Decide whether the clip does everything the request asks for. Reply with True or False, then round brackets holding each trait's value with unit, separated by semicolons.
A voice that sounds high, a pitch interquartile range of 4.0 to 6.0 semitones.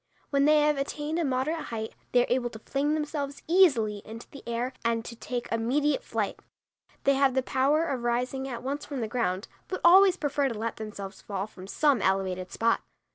True (260 Hz; 4.3 semitones)